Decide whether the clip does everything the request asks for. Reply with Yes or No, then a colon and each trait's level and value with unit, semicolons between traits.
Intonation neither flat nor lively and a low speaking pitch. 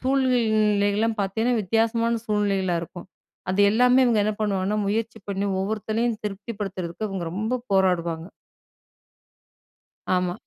No: average, 3.0 semitones; high, 210 Hz